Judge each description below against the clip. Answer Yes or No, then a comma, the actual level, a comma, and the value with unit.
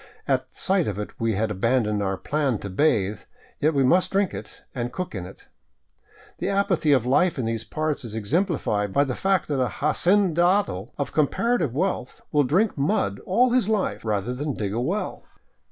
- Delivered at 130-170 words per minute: No, average, 190 wpm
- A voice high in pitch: No, medium, 140 Hz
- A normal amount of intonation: No, wide, 8.4 semitones